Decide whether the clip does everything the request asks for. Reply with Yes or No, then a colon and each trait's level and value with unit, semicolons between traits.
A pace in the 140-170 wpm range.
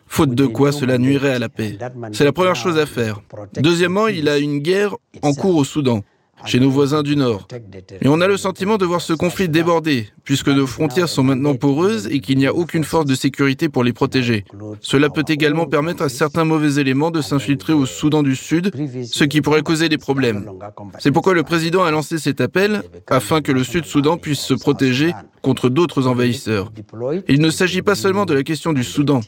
No: average, 215 wpm